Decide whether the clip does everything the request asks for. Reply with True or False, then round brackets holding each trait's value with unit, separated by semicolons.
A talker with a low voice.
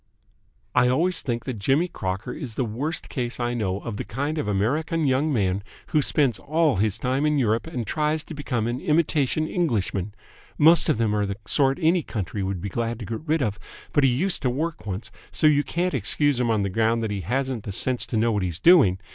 True (125 Hz)